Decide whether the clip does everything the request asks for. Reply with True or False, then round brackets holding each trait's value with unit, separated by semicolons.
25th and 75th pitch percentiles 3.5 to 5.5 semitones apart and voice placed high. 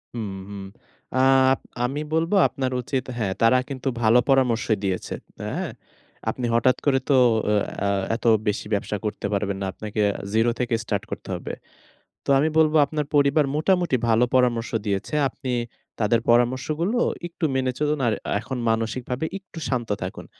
False (4.2 semitones; 125 Hz)